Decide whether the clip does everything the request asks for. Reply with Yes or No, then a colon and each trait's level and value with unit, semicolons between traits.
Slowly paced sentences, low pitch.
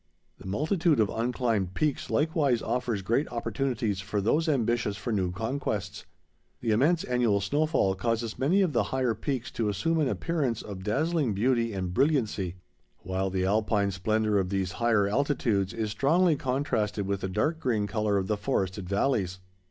No: average, 165 wpm; low, 115 Hz